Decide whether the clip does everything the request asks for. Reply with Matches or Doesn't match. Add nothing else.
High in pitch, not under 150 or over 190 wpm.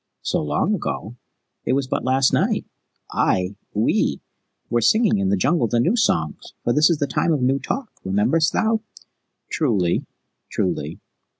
Doesn't match